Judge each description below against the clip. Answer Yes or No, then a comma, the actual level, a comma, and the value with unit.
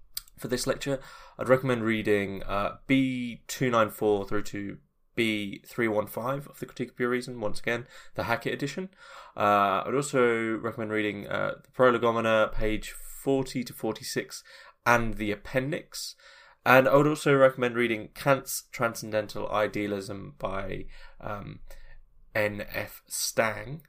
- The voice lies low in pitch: Yes, low, 120 Hz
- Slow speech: Yes, slow, 130 wpm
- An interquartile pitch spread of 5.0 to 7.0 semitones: No, average, 4.0 semitones